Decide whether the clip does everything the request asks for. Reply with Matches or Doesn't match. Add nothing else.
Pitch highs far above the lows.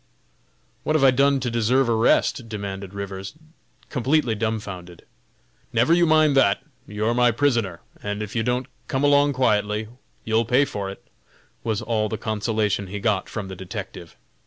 Doesn't match